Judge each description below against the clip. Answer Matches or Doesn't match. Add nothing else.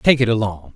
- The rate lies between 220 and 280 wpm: Matches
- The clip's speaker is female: Doesn't match